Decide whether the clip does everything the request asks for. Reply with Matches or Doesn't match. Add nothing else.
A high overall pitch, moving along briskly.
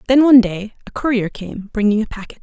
Matches